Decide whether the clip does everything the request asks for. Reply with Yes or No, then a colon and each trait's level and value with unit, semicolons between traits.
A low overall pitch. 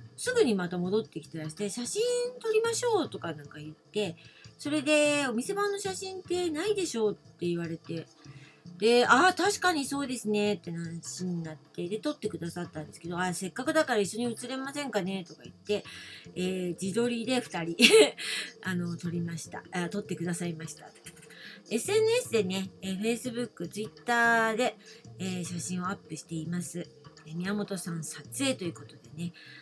No: high, 190 Hz